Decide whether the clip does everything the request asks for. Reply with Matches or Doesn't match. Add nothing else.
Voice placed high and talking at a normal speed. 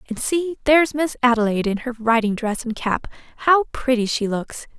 Matches